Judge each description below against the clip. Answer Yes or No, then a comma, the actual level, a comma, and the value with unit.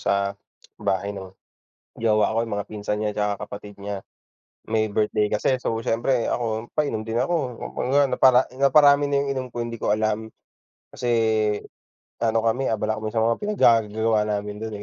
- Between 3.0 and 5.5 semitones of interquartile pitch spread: No, narrow, 2.6 semitones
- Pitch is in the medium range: No, low, 110 Hz